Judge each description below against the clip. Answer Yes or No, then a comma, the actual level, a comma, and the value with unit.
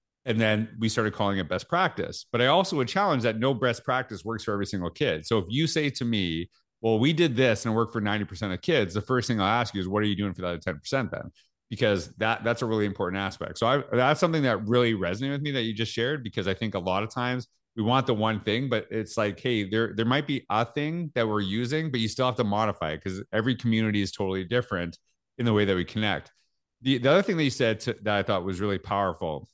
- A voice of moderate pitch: No, low, 110 Hz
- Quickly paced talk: Yes, fast, 270 wpm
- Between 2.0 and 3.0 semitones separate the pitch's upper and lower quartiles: No, average, 3.5 semitones